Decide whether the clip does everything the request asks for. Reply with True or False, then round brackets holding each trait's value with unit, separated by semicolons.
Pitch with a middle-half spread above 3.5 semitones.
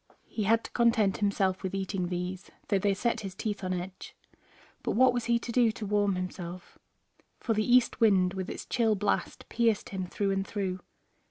False (3.2 semitones)